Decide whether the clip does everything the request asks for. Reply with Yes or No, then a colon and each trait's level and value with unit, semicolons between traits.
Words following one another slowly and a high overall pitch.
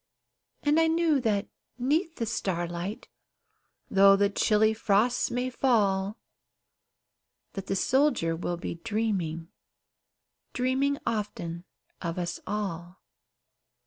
Yes: slow, 105 wpm; high, 210 Hz